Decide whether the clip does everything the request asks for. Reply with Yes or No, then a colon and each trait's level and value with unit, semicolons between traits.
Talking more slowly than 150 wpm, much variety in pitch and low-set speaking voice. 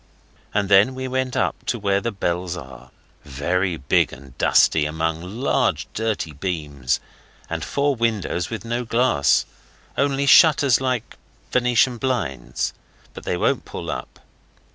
Yes: average, 140 wpm; wide, 7.8 semitones; low, 100 Hz